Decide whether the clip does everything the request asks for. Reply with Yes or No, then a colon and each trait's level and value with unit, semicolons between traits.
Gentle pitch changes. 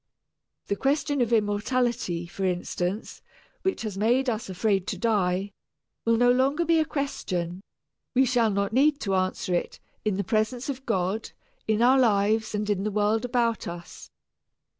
No: average, 4.1 semitones